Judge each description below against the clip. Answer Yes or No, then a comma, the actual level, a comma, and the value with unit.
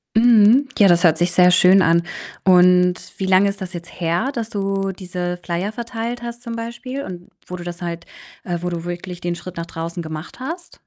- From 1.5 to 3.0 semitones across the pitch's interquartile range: No, average, 4.2 semitones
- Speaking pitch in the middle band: Yes, medium, 180 Hz